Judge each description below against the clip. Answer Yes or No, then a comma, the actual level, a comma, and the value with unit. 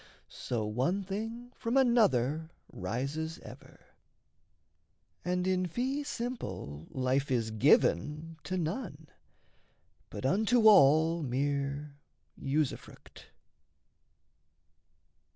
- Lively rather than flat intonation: Yes, wide, 7.0 semitones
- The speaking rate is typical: No, slow, 80 wpm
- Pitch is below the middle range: No, medium, 160 Hz